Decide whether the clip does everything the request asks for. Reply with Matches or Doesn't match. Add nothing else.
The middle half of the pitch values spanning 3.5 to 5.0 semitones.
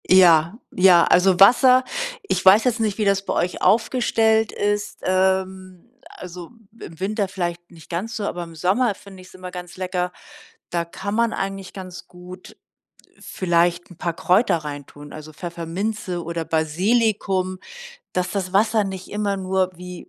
Doesn't match